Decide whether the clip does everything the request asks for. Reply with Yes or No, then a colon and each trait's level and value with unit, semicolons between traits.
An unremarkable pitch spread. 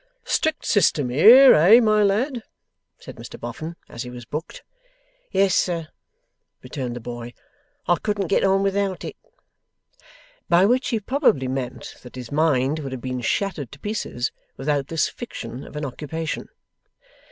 No: wide, 7.6 semitones